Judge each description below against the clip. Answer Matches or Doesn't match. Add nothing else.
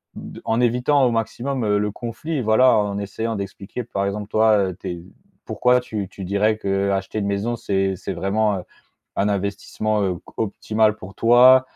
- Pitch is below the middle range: Matches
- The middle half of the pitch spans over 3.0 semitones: Doesn't match